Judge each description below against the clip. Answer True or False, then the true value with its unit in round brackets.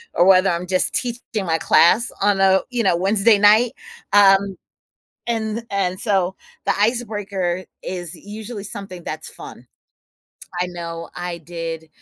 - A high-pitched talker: True (195 Hz)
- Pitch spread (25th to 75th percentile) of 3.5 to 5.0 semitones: False (3.0 semitones)